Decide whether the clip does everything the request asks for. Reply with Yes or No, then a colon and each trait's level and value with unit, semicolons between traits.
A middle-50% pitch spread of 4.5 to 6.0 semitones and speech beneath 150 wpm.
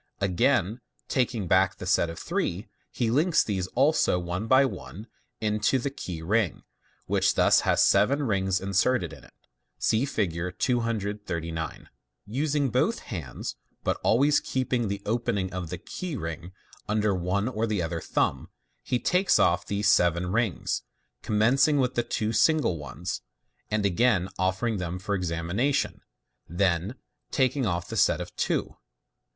No: wide, 5.5 semitones; average, 155 wpm